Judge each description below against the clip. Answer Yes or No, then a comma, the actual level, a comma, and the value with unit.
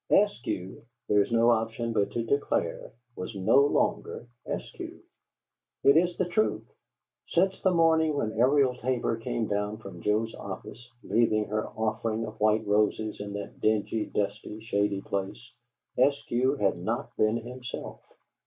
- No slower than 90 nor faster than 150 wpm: Yes, average, 145 wpm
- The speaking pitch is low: Yes, low, 115 Hz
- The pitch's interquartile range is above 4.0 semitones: No, average, 3.4 semitones